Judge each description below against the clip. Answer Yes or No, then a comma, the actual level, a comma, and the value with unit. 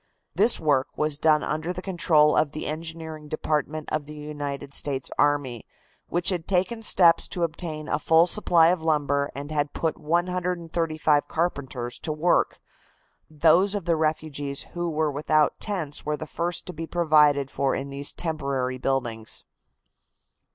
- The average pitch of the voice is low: No, medium, 155 Hz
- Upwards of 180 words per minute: No, average, 155 wpm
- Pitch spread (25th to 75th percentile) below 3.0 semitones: Yes, narrow, 2.6 semitones